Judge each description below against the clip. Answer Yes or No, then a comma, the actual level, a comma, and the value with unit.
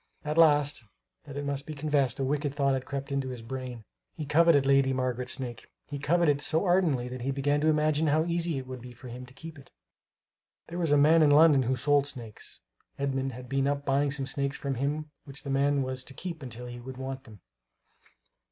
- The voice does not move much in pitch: Yes, narrow, 2.2 semitones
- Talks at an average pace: No, fast, 220 wpm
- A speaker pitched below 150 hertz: Yes, medium, 140 Hz